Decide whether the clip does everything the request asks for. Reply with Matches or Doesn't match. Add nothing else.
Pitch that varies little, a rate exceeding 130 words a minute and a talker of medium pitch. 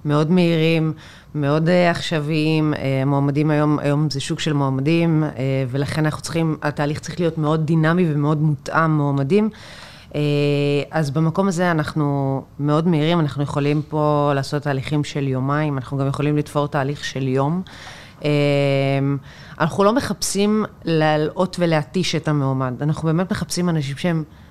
Matches